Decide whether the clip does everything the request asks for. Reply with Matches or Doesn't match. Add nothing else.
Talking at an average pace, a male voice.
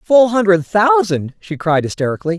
Matches